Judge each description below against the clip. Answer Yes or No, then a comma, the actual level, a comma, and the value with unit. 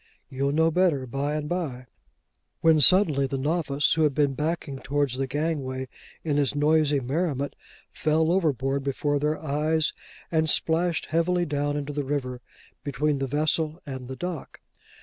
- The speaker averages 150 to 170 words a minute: Yes, average, 155 wpm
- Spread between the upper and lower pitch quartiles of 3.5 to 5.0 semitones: No, narrow, 2.5 semitones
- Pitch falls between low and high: Yes, medium, 145 Hz